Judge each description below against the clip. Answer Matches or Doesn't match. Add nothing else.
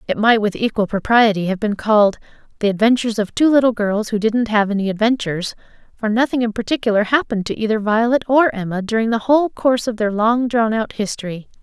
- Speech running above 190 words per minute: Matches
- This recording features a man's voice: Doesn't match